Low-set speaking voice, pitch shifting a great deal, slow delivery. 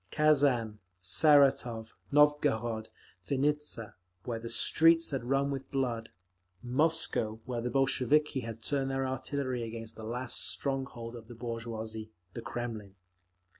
No: low, 120 Hz; average, 3.4 semitones; slow, 120 wpm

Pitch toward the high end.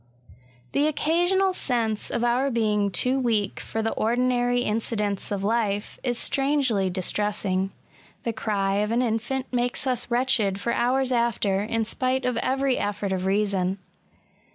Yes: high, 230 Hz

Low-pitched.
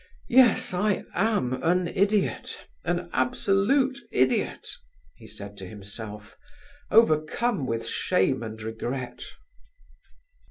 No: medium, 145 Hz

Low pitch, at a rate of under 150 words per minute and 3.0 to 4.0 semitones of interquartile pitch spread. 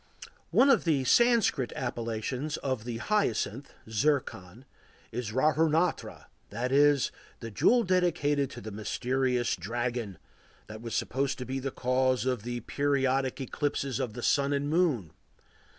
Yes: low, 130 Hz; slow, 135 wpm; average, 3.4 semitones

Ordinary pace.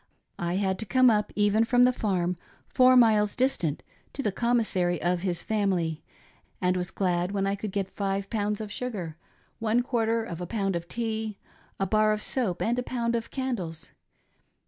Yes: average, 185 wpm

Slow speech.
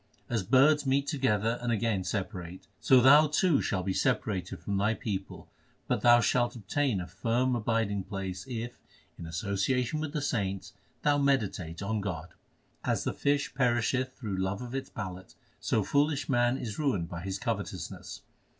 No: average, 165 wpm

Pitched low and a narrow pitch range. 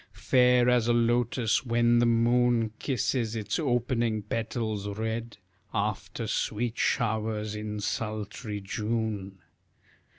Yes: low, 115 Hz; narrow, 2.0 semitones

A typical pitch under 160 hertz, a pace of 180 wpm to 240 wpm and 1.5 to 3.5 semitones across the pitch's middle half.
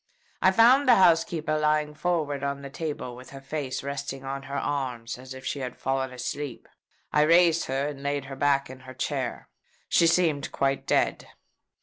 Yes: medium, 140 Hz; average, 185 wpm; narrow, 2.5 semitones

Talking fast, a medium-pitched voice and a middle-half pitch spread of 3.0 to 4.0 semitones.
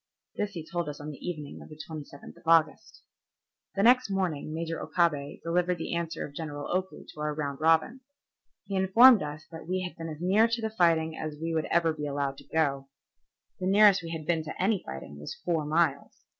Yes: fast, 210 wpm; medium, 165 Hz; average, 3.5 semitones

